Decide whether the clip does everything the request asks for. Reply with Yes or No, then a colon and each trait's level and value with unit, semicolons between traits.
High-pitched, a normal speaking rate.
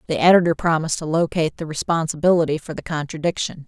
No: medium, 160 Hz; average, 165 wpm